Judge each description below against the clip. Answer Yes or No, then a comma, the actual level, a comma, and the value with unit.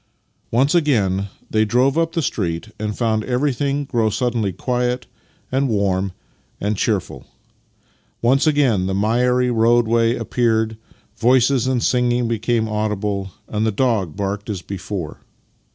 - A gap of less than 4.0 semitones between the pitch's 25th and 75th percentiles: Yes, average, 3.4 semitones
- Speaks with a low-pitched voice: Yes, low, 115 Hz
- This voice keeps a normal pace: No, slow, 130 wpm